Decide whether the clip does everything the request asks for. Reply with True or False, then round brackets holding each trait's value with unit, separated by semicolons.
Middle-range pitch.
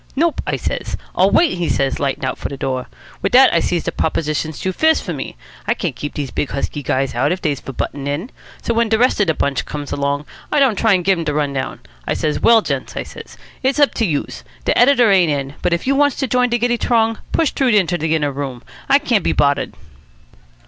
True (170 Hz)